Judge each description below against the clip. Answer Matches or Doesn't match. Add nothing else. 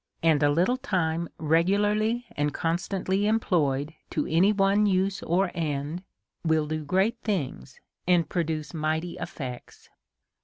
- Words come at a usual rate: Doesn't match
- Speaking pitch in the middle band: Matches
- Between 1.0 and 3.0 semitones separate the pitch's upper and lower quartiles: Doesn't match